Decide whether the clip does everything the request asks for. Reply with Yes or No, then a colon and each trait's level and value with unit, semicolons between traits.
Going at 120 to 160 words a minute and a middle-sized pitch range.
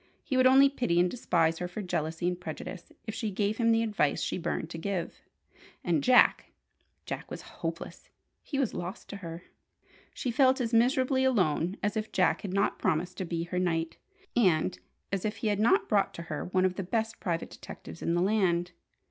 No: average, 200 wpm; average, 4.9 semitones